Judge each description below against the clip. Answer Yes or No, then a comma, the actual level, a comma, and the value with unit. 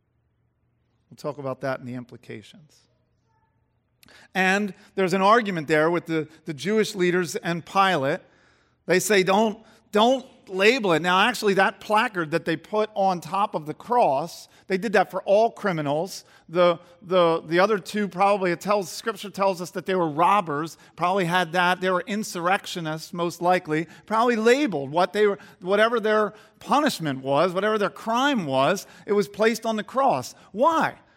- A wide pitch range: No, average, 4.3 semitones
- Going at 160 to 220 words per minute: Yes, average, 165 wpm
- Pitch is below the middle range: No, medium, 185 Hz